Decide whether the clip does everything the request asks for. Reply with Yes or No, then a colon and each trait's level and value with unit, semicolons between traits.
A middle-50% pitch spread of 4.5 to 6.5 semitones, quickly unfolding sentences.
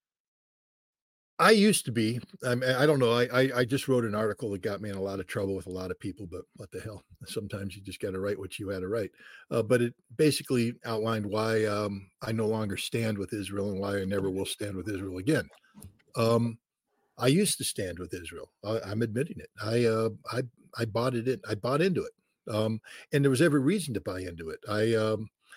No: average, 3.7 semitones; fast, 230 wpm